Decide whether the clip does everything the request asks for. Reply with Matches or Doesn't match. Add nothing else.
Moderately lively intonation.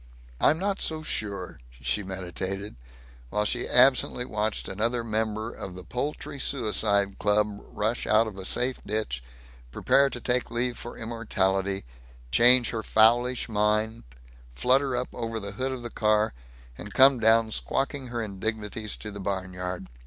Matches